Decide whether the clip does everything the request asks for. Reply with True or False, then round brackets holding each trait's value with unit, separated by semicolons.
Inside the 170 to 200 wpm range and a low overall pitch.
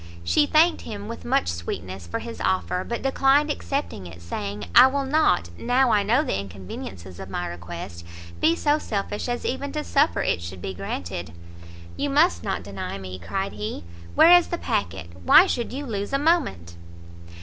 False (180 wpm; 200 Hz)